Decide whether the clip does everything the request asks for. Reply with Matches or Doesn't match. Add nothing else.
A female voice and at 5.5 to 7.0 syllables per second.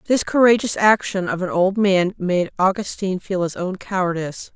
Doesn't match